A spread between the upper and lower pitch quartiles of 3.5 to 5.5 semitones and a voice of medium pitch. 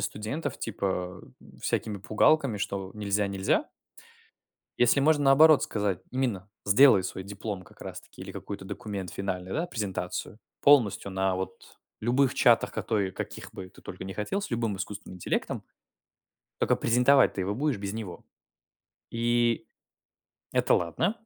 No: average, 4.3 semitones; low, 105 Hz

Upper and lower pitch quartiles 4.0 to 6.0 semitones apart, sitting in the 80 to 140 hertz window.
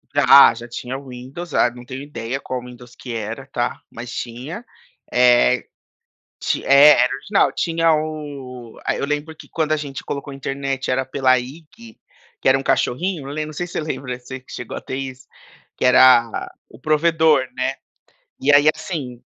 No: average, 3.4 semitones; low, 135 Hz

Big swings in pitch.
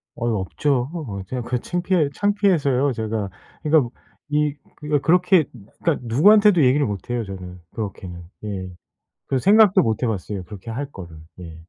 Yes: wide, 8.0 semitones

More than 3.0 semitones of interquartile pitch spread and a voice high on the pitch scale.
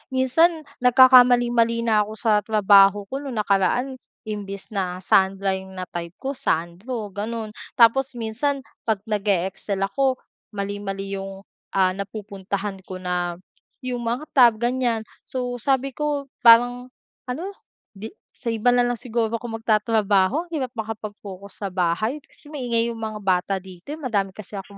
Yes: average, 4.0 semitones; high, 220 Hz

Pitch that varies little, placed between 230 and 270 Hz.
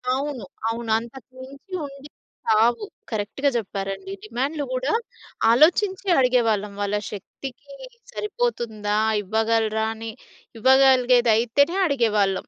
No: average, 4.2 semitones; high, 240 Hz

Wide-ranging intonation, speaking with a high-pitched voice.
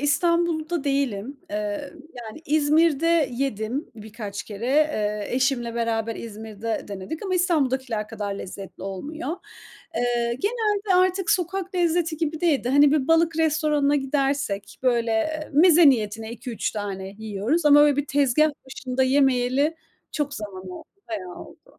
Yes: wide, 6.0 semitones; very high, 270 Hz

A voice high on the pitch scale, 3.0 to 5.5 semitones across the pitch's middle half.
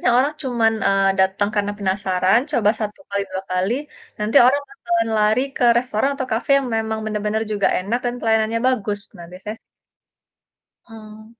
No: high, 215 Hz; narrow, 2.5 semitones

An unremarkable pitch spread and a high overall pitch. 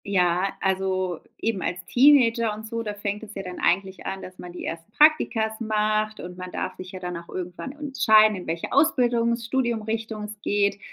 Yes: average, 3.6 semitones; high, 210 Hz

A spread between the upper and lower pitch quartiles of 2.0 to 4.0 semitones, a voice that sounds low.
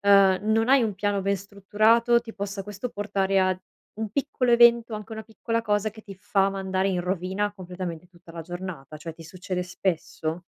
No: average, 2.8 semitones; high, 195 Hz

